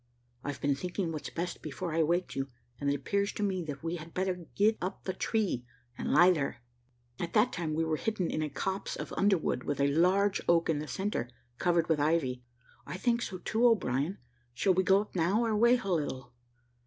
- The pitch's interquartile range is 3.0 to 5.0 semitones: Yes, average, 4.4 semitones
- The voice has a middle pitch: Yes, medium, 175 Hz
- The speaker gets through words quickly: Yes, fast, 215 wpm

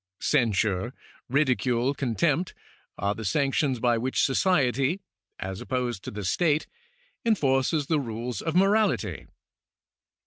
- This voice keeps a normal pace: No, slow, 115 wpm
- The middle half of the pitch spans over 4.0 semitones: Yes, average, 4.7 semitones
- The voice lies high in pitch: No, low, 130 Hz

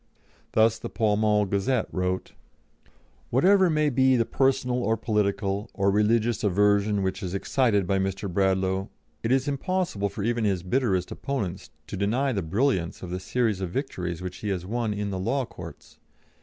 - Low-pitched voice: Yes, low, 105 Hz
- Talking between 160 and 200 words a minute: Yes, average, 170 wpm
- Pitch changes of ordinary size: Yes, average, 4.2 semitones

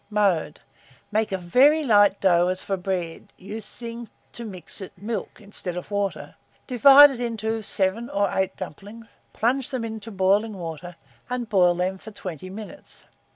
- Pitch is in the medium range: No, high, 205 Hz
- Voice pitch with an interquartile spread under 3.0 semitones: No, average, 3.6 semitones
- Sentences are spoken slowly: No, average, 155 wpm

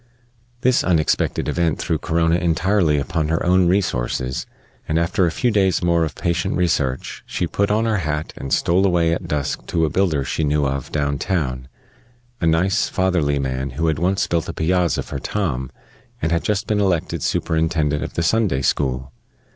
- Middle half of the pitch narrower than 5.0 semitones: Yes, average, 3.8 semitones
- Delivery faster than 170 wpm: Yes, average, 180 wpm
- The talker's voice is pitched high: No, very low, 80 Hz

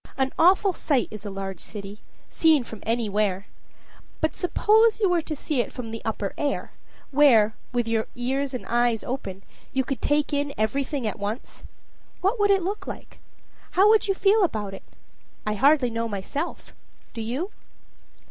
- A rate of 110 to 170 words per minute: No, average, 180 wpm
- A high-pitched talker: Yes, very high, 255 Hz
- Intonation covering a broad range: Yes, wide, 6.7 semitones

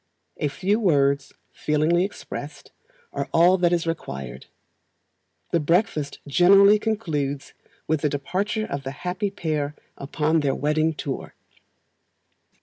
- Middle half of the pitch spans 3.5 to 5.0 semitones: Yes, average, 4.4 semitones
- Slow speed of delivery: Yes, slow, 120 wpm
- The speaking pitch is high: No, medium, 160 Hz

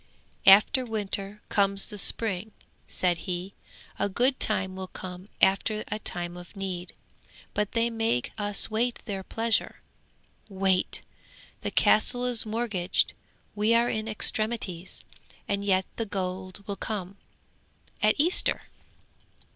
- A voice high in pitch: Yes, high, 200 Hz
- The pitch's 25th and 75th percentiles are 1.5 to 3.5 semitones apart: Yes, average, 2.8 semitones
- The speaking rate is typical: No, slow, 125 wpm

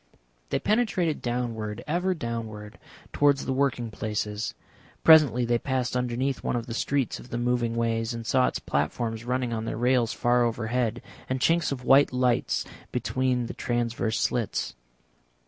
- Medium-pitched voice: No, low, 120 Hz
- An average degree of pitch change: No, narrow, 2.2 semitones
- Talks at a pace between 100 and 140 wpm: No, average, 155 wpm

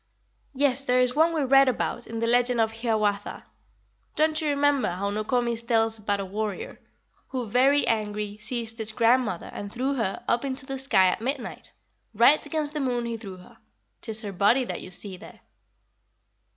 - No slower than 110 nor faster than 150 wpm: No, average, 185 wpm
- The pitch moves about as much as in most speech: Yes, average, 4.0 semitones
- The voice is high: Yes, high, 235 Hz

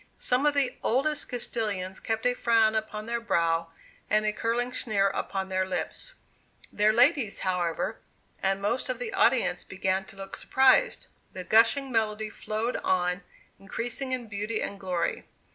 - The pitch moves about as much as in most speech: Yes, average, 4.0 semitones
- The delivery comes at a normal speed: Yes, average, 155 wpm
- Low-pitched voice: No, high, 215 Hz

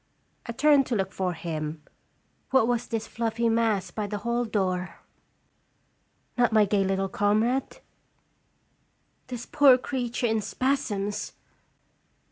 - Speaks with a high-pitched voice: Yes, high, 220 Hz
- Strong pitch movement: No, average, 3.9 semitones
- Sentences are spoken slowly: Yes, slow, 120 wpm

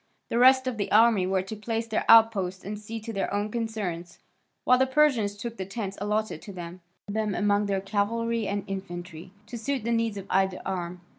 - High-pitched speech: Yes, high, 210 Hz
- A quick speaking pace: Yes, fast, 215 wpm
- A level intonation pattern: No, average, 3.0 semitones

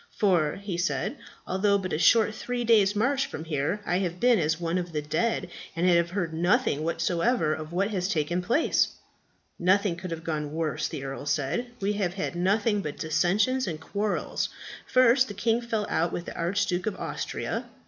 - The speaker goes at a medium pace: Yes, average, 190 wpm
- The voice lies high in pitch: No, medium, 180 Hz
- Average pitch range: Yes, average, 4.2 semitones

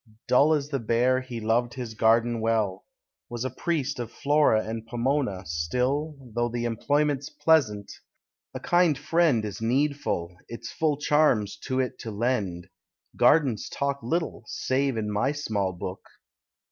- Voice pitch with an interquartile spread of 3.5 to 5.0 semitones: Yes, average, 4.5 semitones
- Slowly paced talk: No, average, 145 wpm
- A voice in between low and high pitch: No, low, 120 Hz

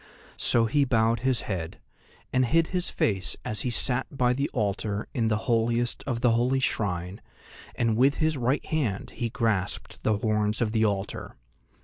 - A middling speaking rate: Yes, average, 170 wpm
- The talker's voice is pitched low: Yes, low, 115 Hz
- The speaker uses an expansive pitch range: No, average, 3.1 semitones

